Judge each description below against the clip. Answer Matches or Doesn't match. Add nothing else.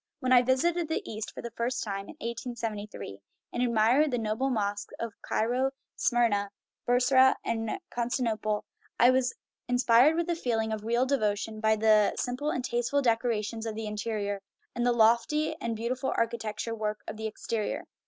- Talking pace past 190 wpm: Doesn't match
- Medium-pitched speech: Doesn't match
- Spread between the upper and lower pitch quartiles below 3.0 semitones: Matches